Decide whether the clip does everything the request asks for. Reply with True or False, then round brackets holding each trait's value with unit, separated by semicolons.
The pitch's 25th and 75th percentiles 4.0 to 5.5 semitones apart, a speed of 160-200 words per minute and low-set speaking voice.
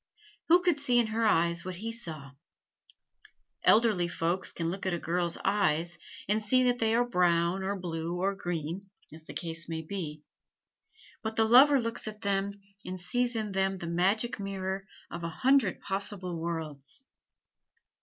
False (4.5 semitones; 165 wpm; 190 Hz)